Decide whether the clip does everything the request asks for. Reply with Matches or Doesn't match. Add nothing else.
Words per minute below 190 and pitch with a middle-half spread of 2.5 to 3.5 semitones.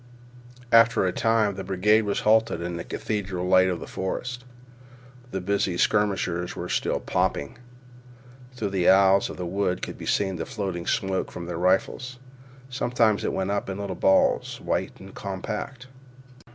Matches